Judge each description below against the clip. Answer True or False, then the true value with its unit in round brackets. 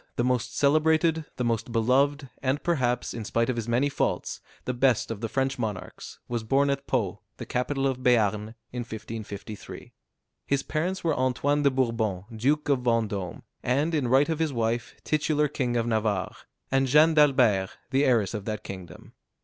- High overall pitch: False (125 Hz)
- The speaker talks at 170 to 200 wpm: True (175 wpm)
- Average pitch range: True (3.9 semitones)